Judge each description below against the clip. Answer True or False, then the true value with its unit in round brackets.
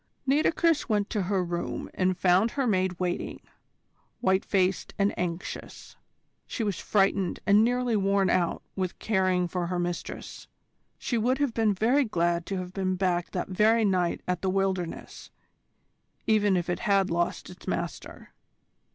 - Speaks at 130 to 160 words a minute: True (155 wpm)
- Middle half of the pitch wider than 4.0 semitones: False (3.0 semitones)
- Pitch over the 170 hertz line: True (190 Hz)